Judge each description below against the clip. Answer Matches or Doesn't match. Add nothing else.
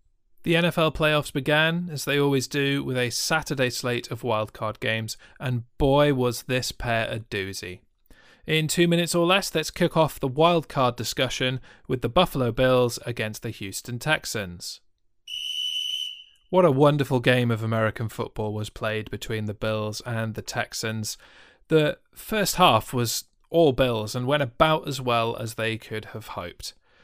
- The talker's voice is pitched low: Matches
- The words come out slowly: Doesn't match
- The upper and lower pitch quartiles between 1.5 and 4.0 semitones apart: Doesn't match